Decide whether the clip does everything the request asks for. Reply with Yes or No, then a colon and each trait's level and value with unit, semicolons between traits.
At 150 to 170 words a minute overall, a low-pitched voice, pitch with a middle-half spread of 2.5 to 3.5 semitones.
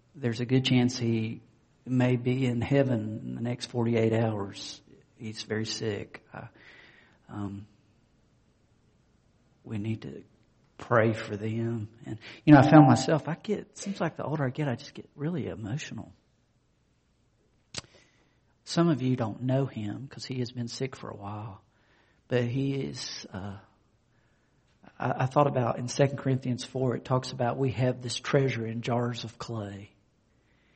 Yes: average, 160 wpm; low, 120 Hz; average, 2.9 semitones